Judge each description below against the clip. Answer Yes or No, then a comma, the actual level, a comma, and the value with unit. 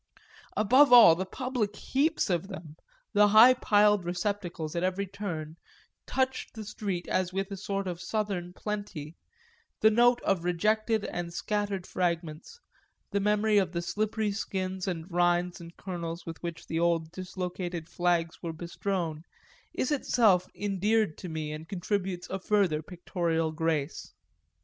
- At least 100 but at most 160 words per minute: Yes, average, 150 wpm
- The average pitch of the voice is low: No, medium, 185 Hz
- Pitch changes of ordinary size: Yes, average, 3.4 semitones